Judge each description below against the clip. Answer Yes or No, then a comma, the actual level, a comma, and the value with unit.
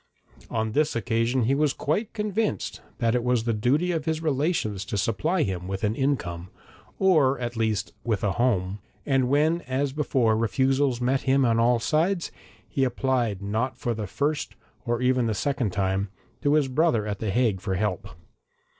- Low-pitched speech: Yes, low, 125 Hz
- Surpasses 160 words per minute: Yes, average, 180 wpm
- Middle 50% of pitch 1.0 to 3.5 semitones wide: No, average, 4.8 semitones